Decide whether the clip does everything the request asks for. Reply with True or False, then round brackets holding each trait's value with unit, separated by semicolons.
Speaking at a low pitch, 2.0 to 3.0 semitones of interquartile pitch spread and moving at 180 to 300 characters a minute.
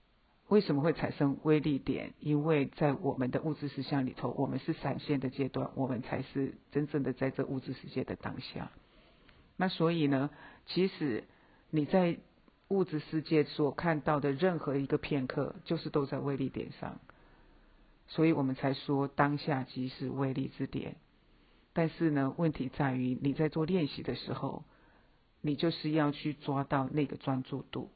False (145 Hz; 2.5 semitones; 250 characters per minute)